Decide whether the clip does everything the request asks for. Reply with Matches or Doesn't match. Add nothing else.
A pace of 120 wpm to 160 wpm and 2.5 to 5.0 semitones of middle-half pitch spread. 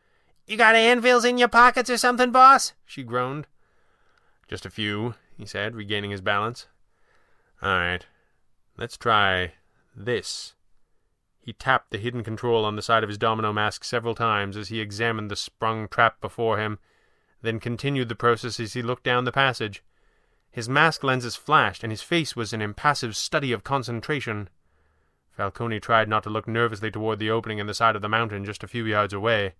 Doesn't match